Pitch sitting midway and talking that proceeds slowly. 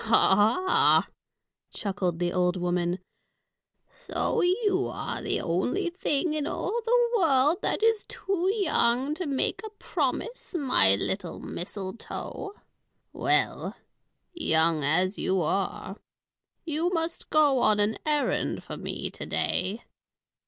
No: very high, 270 Hz; slow, 125 wpm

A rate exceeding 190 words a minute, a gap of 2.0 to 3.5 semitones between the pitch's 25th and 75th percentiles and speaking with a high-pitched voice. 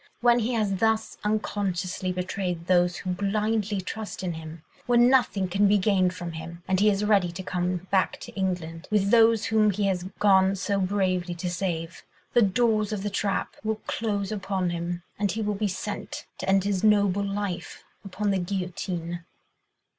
No: average, 180 wpm; narrow, 2.6 semitones; high, 195 Hz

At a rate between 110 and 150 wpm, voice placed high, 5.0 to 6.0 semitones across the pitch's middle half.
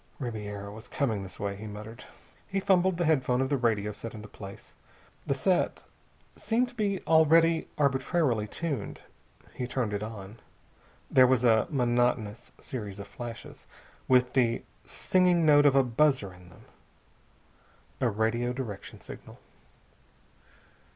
No: average, 140 wpm; low, 125 Hz; wide, 5.5 semitones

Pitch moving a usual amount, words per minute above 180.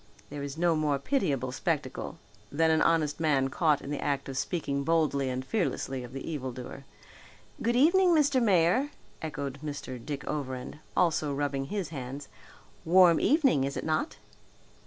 No: average, 3.8 semitones; average, 160 wpm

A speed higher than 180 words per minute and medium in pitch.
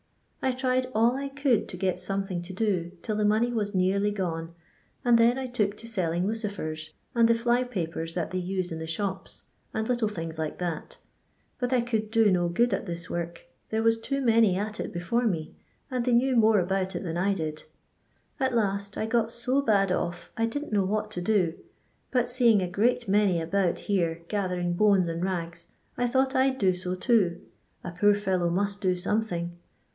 No: fast, 205 wpm; high, 200 Hz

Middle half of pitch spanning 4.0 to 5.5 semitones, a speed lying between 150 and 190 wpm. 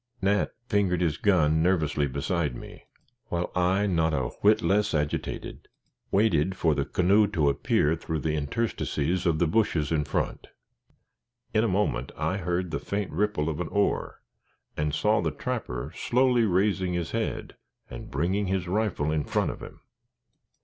Yes: average, 4.7 semitones; average, 160 wpm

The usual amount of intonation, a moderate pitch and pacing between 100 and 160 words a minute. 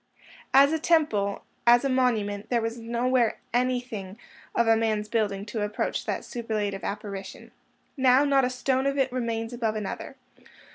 No: average, 3.3 semitones; high, 235 Hz; average, 150 wpm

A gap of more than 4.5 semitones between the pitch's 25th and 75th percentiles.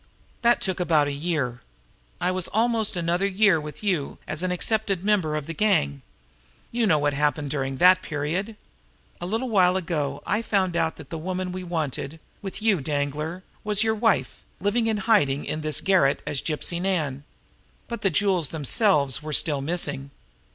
Yes: average, 5.0 semitones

